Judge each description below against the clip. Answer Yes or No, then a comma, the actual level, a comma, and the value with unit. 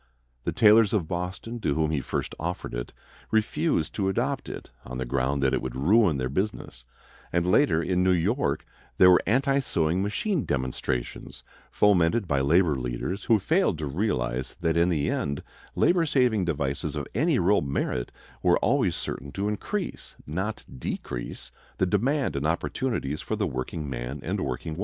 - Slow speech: No, average, 165 wpm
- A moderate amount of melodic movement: No, wide, 7.2 semitones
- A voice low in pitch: Yes, very low, 85 Hz